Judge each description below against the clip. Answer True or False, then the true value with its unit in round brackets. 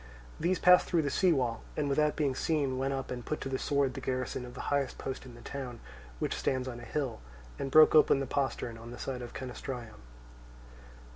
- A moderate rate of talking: False (220 wpm)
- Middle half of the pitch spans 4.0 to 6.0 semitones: False (2.5 semitones)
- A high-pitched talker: False (135 Hz)